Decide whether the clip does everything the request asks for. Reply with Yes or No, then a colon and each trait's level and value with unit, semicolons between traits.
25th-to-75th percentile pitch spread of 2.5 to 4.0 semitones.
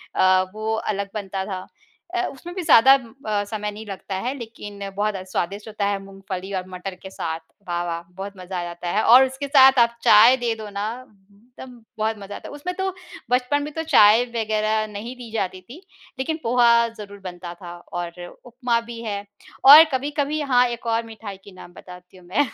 No: average, 4.4 semitones